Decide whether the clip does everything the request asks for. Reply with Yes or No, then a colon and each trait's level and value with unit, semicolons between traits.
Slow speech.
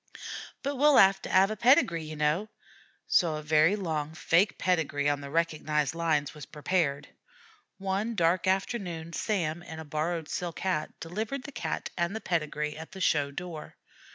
No: average, 170 wpm